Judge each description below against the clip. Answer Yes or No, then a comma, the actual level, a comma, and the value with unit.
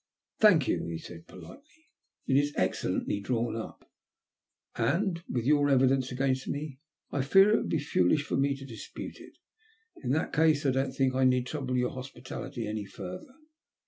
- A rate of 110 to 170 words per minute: No, average, 180 wpm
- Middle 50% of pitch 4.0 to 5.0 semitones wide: No, average, 3.3 semitones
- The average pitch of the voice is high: No, low, 135 Hz